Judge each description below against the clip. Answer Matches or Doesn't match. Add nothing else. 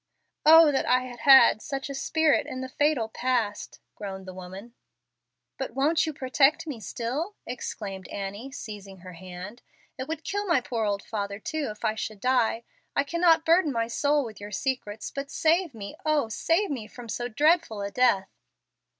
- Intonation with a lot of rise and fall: Matches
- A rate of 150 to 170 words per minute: Doesn't match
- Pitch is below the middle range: Doesn't match